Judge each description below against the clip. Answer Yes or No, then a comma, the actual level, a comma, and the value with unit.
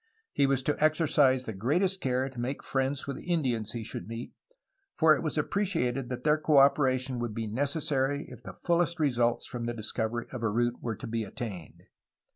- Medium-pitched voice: No, low, 130 Hz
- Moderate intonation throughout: Yes, average, 4.0 semitones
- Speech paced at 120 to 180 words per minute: No, average, 200 wpm